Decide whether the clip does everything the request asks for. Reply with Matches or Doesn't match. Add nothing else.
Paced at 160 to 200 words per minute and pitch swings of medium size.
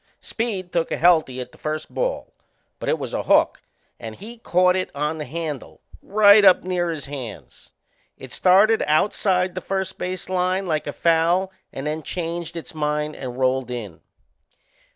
Matches